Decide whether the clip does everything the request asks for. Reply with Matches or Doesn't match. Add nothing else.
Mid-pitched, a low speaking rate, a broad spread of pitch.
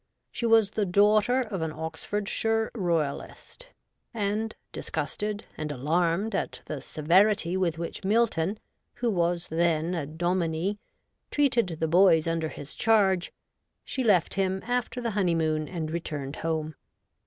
Doesn't match